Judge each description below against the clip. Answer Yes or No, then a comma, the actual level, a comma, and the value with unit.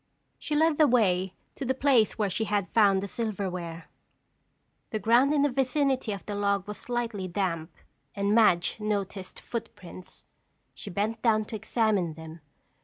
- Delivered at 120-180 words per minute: Yes, average, 160 wpm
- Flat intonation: No, average, 4.0 semitones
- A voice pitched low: No, high, 210 Hz